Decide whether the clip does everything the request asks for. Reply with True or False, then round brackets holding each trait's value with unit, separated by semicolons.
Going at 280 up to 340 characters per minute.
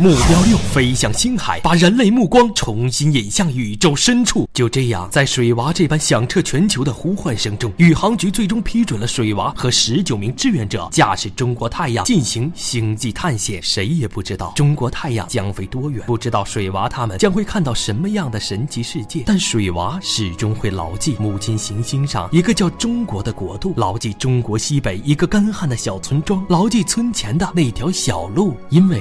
True (300 characters per minute)